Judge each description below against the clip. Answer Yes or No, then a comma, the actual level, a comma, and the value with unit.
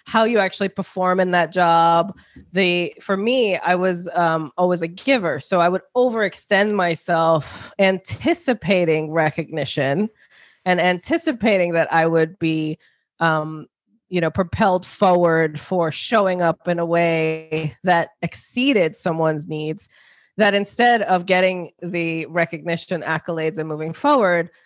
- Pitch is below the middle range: No, medium, 175 Hz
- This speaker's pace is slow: Yes, slow, 130 wpm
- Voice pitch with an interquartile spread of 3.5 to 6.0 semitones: No, average, 3.0 semitones